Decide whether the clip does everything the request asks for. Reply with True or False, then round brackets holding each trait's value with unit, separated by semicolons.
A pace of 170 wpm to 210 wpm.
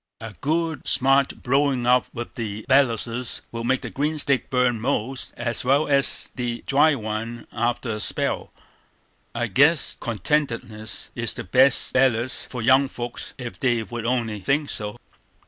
False (155 wpm)